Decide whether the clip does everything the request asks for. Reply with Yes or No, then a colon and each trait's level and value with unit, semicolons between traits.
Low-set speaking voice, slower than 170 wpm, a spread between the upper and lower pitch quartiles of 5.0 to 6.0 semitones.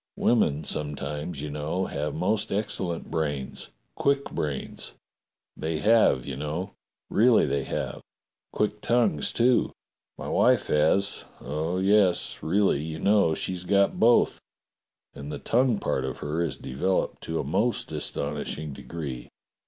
Yes: very low, 80 Hz; average, 140 wpm; wide, 5.5 semitones